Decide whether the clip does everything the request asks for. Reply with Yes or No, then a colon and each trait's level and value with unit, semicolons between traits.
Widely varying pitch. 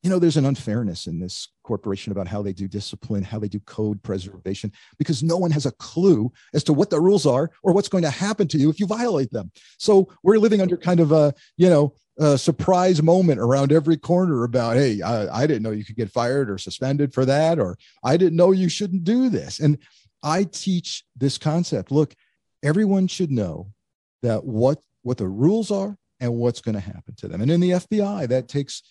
Yes: wide, 8.0 semitones